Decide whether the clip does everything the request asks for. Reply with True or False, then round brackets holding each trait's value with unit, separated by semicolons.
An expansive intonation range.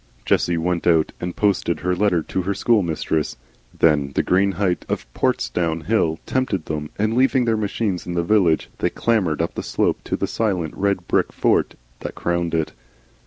False (3.8 semitones)